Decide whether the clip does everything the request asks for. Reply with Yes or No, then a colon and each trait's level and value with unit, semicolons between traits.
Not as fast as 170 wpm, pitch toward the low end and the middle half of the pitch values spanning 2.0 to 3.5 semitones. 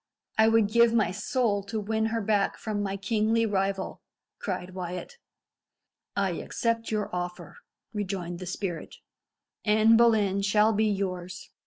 No: average, 140 wpm; high, 205 Hz; average, 2.7 semitones